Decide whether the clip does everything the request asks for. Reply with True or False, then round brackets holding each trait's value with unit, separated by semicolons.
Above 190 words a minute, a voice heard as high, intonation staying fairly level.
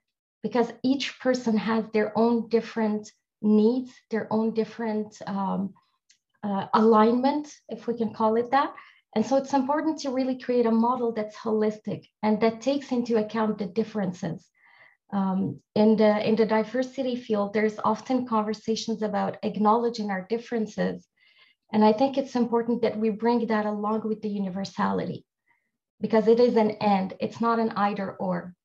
False (155 wpm; 220 Hz; 1.9 semitones)